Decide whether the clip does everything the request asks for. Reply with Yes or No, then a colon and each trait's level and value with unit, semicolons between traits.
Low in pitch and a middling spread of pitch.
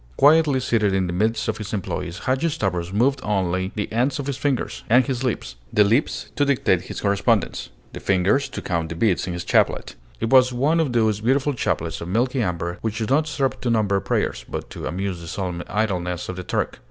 No: low, 110 Hz; wide, 6.1 semitones